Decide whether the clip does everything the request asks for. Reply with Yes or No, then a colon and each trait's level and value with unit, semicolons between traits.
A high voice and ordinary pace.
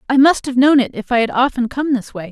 No: very high, 255 Hz; fast, 310 wpm